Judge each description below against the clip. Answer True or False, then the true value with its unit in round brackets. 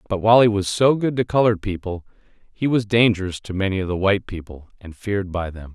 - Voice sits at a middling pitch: False (100 Hz)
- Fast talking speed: True (230 wpm)